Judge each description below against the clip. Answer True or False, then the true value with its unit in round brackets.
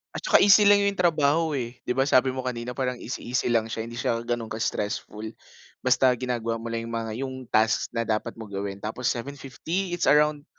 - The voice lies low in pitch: True (120 Hz)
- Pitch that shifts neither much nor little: True (3.7 semitones)